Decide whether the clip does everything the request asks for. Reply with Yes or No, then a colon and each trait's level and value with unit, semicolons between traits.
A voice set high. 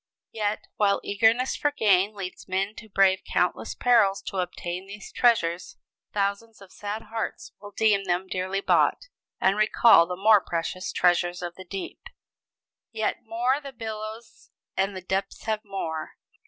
Yes: high, 200 Hz